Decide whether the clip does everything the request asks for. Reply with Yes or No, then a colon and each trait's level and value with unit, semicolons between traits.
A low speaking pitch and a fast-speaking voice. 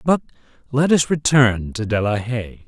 No: low, 120 Hz; average, 180 wpm